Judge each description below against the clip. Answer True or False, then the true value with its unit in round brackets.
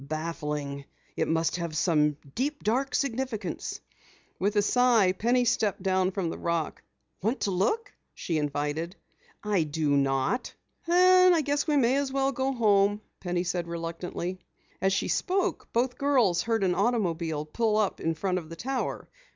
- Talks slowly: False (160 wpm)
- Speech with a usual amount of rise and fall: False (7.0 semitones)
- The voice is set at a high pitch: True (195 Hz)